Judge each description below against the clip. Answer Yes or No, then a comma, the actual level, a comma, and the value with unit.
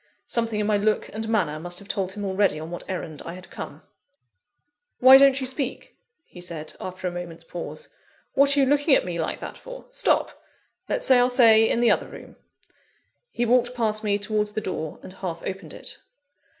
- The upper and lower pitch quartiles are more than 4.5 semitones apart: Yes, wide, 5.6 semitones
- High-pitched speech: Yes, high, 210 Hz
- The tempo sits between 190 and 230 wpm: Yes, average, 200 wpm